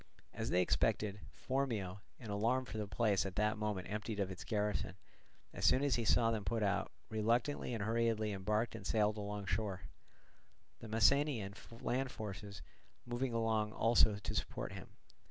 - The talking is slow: No, average, 165 wpm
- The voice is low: Yes, low, 110 Hz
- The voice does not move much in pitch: Yes, narrow, 2.3 semitones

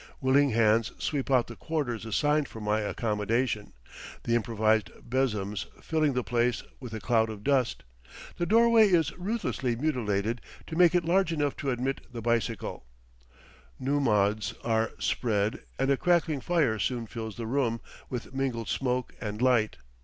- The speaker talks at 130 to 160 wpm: Yes, average, 155 wpm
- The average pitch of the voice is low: Yes, low, 120 Hz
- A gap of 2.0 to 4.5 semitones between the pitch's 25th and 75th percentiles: Yes, average, 4.2 semitones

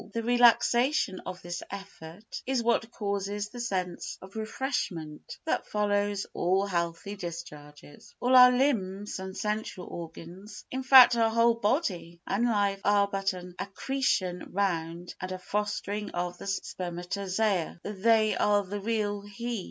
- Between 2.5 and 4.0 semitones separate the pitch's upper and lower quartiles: Yes, average, 3.6 semitones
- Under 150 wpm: Yes, average, 140 wpm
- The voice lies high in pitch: Yes, high, 200 Hz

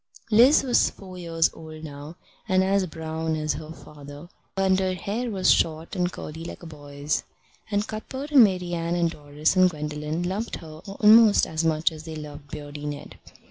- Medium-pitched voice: Yes, medium, 165 Hz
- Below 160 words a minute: No, average, 180 wpm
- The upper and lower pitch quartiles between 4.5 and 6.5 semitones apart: No, average, 3.7 semitones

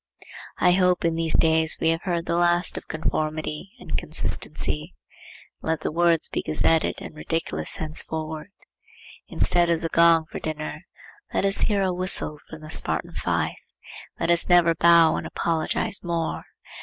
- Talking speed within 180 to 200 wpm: No, average, 155 wpm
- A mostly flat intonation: Yes, narrow, 1.6 semitones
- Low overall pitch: No, medium, 165 Hz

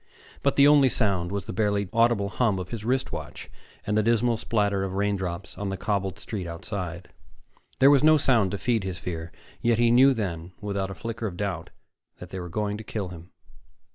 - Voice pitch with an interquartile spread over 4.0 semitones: No, average, 3.7 semitones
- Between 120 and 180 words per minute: No, fast, 205 wpm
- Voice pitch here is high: No, low, 100 Hz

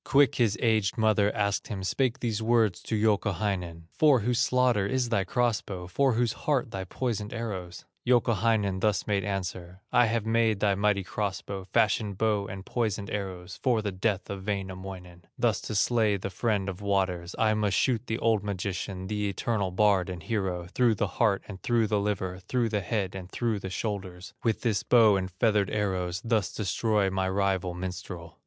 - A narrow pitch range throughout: No, average, 3.0 semitones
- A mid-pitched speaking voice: No, low, 100 Hz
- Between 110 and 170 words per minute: No, average, 185 wpm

